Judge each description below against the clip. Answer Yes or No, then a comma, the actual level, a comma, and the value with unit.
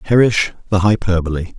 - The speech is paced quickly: No, slow, 115 wpm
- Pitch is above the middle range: No, very low, 95 Hz